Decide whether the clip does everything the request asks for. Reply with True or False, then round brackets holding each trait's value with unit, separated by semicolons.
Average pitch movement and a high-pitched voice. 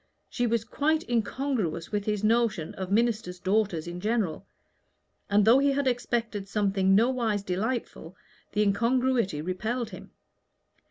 True (3.8 semitones; 215 Hz)